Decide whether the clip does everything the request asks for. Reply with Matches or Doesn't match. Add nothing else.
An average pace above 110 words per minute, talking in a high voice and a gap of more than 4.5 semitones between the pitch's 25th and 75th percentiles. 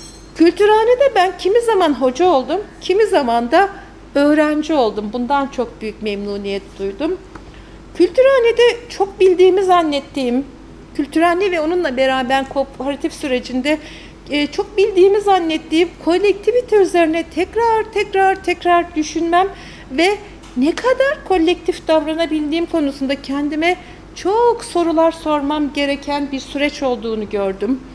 Doesn't match